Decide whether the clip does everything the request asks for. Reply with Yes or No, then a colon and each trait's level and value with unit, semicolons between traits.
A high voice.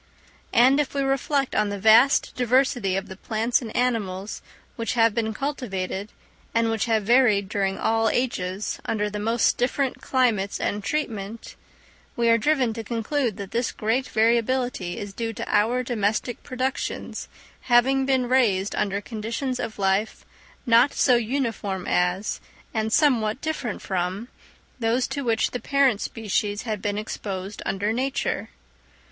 Yes: high, 225 Hz